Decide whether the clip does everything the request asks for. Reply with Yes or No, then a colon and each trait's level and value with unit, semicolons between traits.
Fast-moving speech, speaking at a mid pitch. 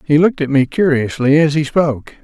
Yes: fast, 215 wpm; medium, 150 Hz